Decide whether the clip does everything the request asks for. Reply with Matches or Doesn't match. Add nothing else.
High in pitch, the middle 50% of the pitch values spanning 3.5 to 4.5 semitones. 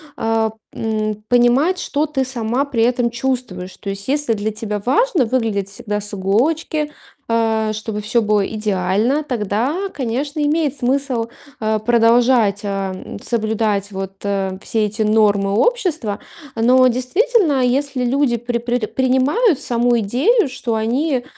Matches